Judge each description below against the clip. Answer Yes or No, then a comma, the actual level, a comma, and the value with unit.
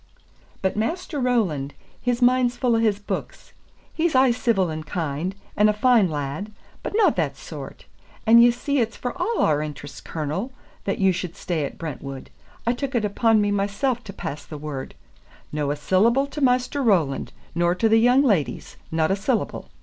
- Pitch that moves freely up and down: Yes, wide, 7.5 semitones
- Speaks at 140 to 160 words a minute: No, average, 185 wpm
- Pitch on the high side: Yes, high, 210 Hz